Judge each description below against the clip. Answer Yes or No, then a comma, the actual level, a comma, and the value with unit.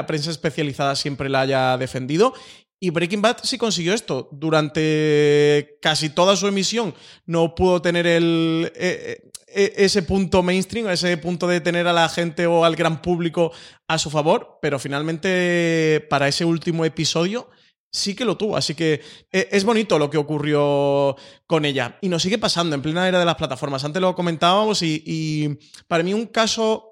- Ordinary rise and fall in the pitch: Yes, average, 3.5 semitones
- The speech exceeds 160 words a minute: Yes, average, 175 wpm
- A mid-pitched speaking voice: Yes, medium, 165 Hz